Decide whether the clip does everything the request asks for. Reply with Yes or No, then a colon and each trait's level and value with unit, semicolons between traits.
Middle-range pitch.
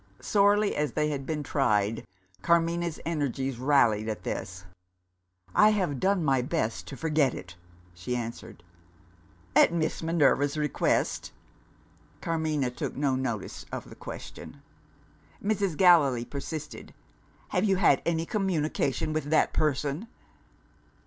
Yes: medium, 150 Hz